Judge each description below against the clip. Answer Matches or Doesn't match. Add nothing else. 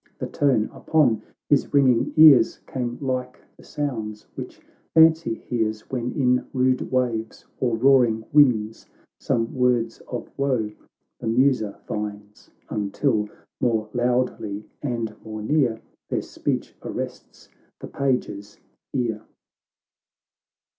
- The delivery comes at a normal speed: Doesn't match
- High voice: Doesn't match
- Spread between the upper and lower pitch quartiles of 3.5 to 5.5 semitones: Doesn't match